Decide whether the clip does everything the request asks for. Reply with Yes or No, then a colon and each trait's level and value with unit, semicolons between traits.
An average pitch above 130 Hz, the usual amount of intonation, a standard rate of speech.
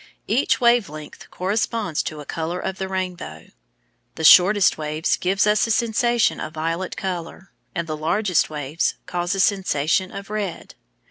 Yes: medium, 185 Hz; average, 4.3 semitones; average, 155 wpm